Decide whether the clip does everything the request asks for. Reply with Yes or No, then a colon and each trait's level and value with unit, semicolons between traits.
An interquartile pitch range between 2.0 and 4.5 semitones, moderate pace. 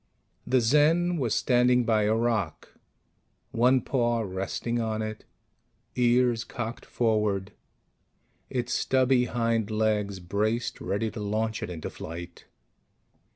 No: narrow, 2.5 semitones; slow, 115 wpm